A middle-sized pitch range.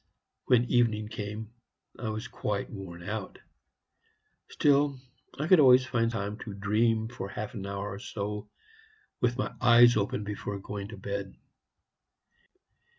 Yes: average, 3.0 semitones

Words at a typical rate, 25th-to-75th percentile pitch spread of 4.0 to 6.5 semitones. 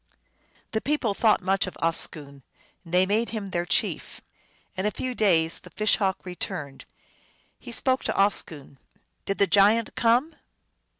Yes: average, 160 wpm; average, 4.5 semitones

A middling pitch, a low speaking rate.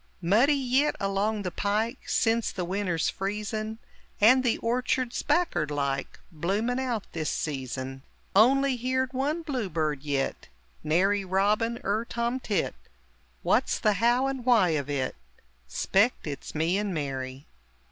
No: high, 205 Hz; slow, 130 wpm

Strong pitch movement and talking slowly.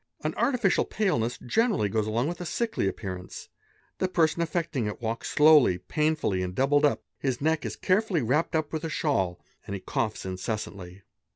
No: wide, 7.9 semitones; average, 175 wpm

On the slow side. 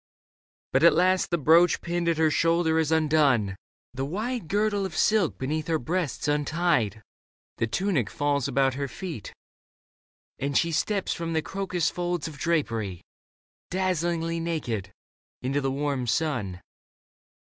No: average, 145 wpm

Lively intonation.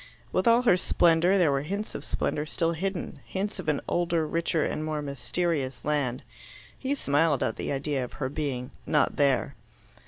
No: average, 3.9 semitones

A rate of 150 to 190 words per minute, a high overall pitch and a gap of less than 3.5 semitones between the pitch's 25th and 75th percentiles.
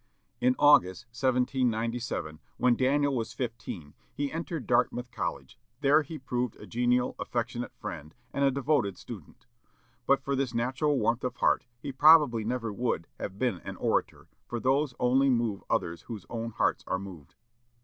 No: average, 160 wpm; low, 125 Hz; average, 3.0 semitones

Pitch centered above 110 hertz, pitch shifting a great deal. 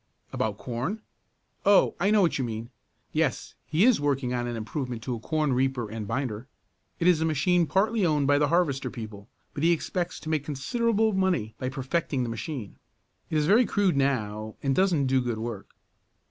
Yes: medium, 140 Hz; wide, 6.3 semitones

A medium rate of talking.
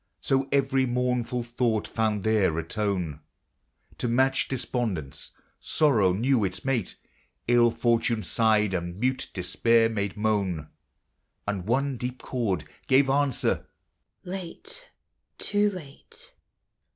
No: slow, 120 wpm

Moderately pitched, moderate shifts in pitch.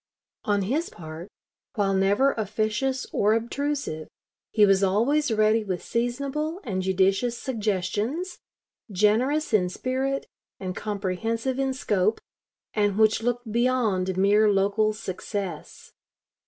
No: high, 215 Hz; average, 4.7 semitones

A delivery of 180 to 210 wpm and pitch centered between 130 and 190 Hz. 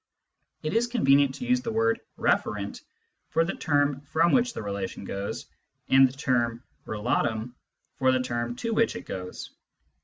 No: average, 160 wpm; low, 135 Hz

